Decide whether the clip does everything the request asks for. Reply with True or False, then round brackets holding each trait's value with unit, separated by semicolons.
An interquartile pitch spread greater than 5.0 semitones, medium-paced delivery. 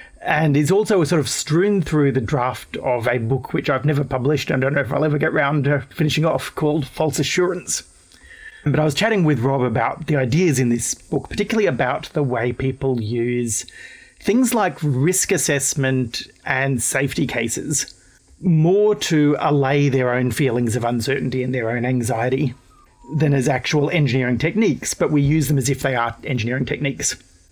False (3.4 semitones; 180 wpm)